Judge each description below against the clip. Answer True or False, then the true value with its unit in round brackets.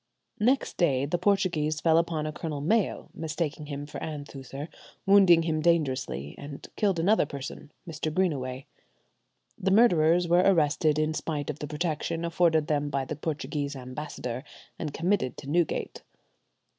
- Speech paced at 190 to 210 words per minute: False (145 wpm)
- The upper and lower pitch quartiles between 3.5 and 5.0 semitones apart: False (2.9 semitones)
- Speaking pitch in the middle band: True (155 Hz)